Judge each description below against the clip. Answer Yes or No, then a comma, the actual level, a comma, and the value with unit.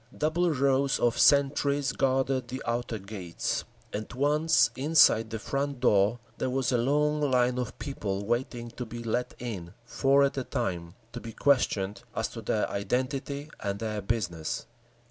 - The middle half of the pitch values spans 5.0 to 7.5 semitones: No, average, 4.2 semitones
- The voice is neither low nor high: No, low, 125 Hz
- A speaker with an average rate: Yes, average, 160 wpm